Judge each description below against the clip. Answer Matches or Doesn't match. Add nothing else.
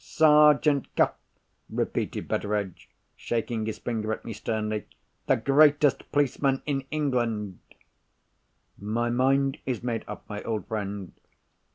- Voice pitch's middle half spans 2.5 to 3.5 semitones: Doesn't match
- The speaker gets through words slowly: Matches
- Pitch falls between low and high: Doesn't match